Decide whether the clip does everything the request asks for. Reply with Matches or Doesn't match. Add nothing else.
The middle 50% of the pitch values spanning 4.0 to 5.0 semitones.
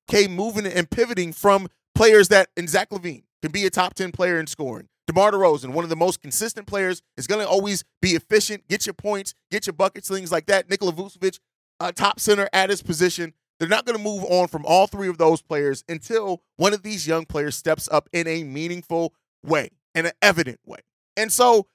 Doesn't match